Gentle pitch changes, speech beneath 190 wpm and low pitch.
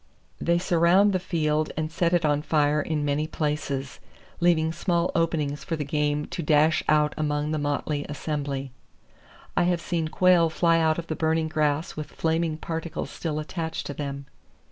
No: narrow, 2.1 semitones; average, 170 wpm; medium, 155 Hz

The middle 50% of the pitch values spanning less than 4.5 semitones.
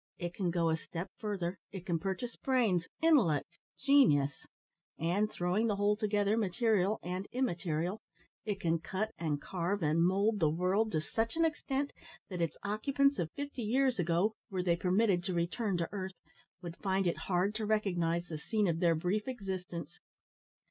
Yes: average, 4.0 semitones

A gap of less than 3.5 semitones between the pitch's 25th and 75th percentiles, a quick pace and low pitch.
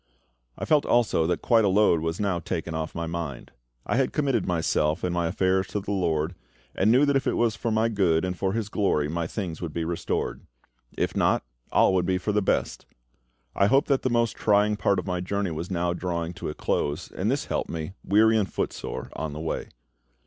No: average, 4.2 semitones; fast, 220 wpm; very low, 95 Hz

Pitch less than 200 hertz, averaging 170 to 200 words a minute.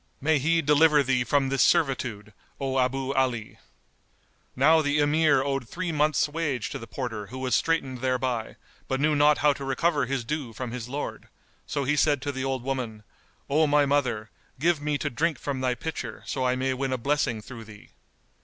Yes: low, 135 Hz; average, 195 wpm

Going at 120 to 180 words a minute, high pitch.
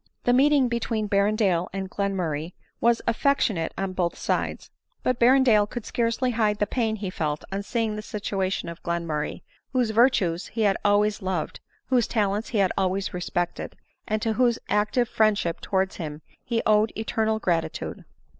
Yes: average, 160 wpm; high, 210 Hz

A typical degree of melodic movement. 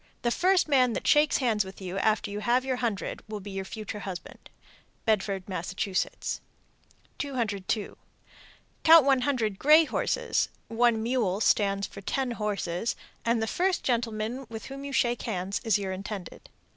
Yes: average, 4.2 semitones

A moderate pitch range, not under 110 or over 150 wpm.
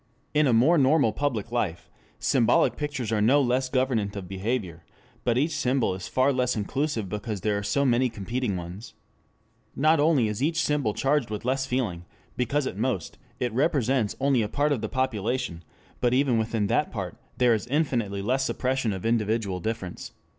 No: average, 4.2 semitones; average, 180 wpm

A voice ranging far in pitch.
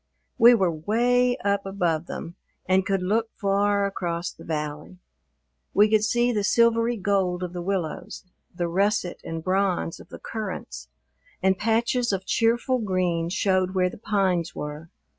No: average, 3.7 semitones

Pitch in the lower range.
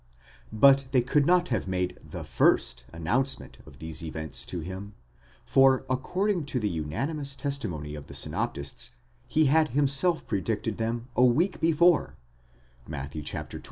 Yes: low, 125 Hz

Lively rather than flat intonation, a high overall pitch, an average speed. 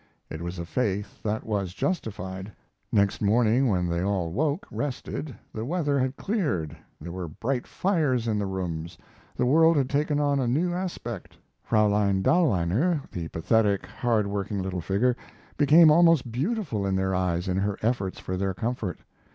No: wide, 6.9 semitones; low, 110 Hz; average, 165 wpm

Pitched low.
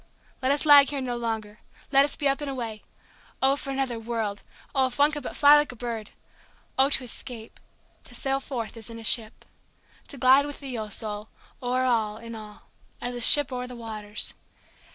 No: high, 245 Hz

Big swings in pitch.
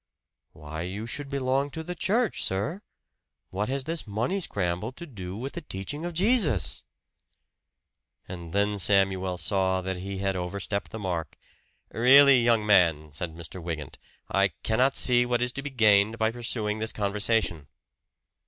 Yes: wide, 5.7 semitones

